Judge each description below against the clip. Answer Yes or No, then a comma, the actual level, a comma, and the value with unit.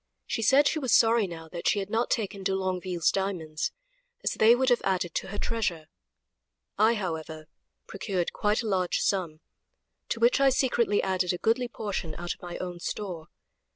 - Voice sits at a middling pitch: No, high, 195 Hz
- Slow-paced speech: No, average, 180 wpm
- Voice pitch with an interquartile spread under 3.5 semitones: No, average, 4.5 semitones